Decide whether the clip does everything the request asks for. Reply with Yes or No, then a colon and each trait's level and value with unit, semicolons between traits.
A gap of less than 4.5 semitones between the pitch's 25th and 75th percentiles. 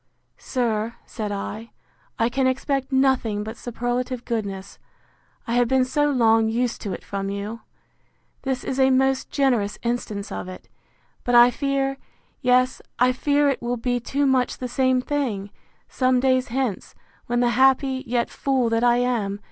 Yes: narrow, 2.6 semitones